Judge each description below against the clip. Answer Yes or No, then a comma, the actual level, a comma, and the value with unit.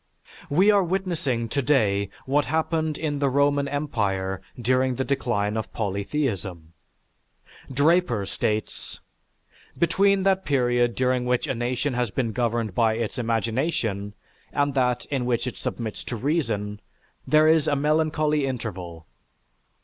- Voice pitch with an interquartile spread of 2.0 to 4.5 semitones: No, average, 4.9 semitones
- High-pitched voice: No, low, 125 Hz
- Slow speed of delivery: Yes, slow, 130 wpm